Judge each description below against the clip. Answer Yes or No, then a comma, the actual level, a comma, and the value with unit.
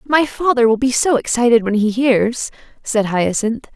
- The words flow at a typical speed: Yes, average, 175 wpm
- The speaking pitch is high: Yes, high, 240 Hz